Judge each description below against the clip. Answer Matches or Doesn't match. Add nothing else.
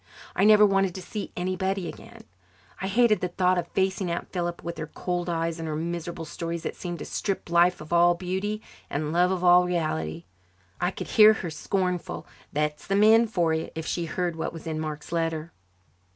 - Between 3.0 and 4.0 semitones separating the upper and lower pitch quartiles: Doesn't match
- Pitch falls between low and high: Matches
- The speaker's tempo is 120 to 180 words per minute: Doesn't match